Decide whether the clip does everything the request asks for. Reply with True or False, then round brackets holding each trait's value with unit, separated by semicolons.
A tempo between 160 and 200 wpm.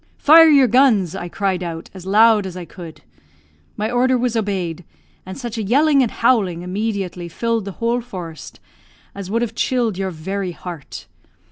True (170 wpm)